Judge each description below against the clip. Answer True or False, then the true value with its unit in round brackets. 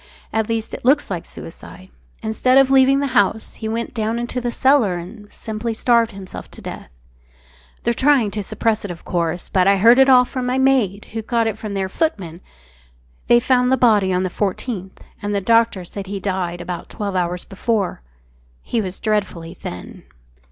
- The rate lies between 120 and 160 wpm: False (195 wpm)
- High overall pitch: True (215 Hz)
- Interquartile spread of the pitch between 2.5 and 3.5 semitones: False (4.2 semitones)